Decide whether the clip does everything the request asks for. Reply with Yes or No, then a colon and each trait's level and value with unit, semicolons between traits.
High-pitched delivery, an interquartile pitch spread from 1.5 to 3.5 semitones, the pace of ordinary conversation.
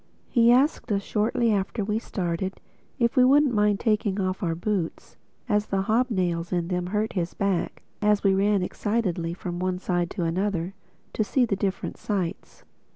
Yes: high, 200 Hz; average, 3.1 semitones; average, 170 wpm